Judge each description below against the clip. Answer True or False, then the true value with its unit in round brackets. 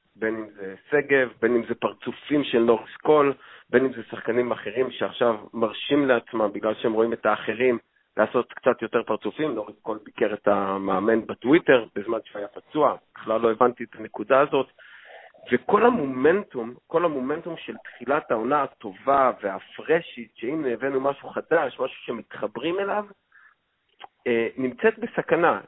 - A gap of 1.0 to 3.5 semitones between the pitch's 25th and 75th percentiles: False (4.4 semitones)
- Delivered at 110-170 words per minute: True (145 wpm)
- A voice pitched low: True (125 Hz)